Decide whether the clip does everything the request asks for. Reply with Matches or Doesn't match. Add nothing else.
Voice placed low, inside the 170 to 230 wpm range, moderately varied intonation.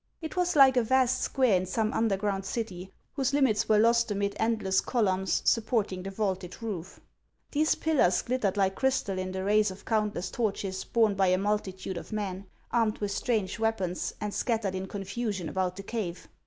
Doesn't match